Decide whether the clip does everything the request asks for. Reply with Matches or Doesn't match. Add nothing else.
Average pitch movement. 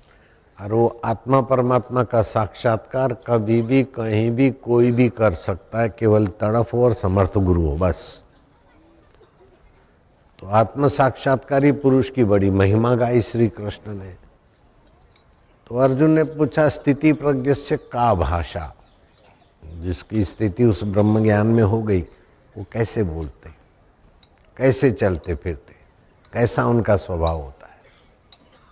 Matches